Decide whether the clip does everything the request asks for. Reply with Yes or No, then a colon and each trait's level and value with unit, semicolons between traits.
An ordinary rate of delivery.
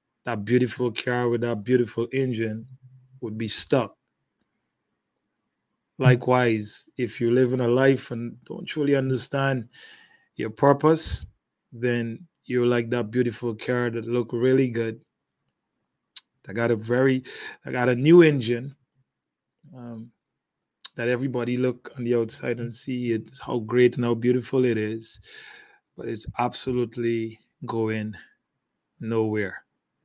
No: slow, 130 wpm